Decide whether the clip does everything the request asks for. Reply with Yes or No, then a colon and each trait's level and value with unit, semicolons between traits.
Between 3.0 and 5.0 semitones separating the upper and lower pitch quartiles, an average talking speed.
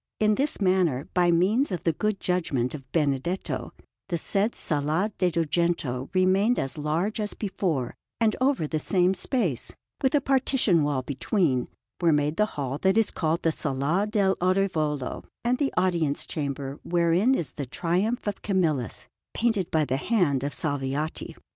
No: wide, 5.5 semitones; average, 160 wpm